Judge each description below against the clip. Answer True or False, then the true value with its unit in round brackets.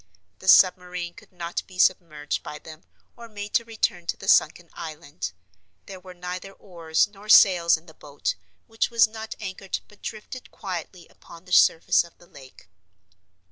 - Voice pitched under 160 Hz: False (180 Hz)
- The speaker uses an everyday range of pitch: True (3.3 semitones)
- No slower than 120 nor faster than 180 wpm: True (170 wpm)